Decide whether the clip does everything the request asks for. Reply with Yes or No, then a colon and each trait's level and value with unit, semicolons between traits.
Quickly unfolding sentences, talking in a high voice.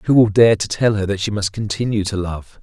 No: fast, 275 wpm; low, 105 Hz